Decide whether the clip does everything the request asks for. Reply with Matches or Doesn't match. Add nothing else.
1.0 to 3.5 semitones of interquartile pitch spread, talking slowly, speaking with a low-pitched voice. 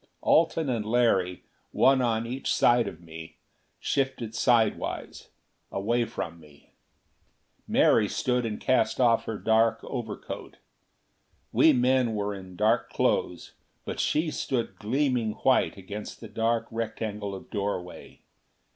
Matches